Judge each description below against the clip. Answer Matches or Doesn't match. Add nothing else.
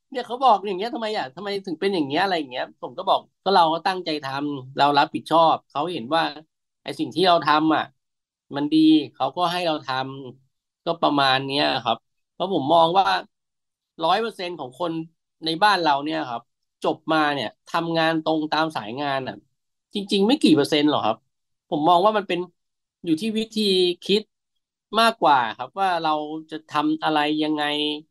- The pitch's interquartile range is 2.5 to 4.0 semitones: Doesn't match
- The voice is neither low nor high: Matches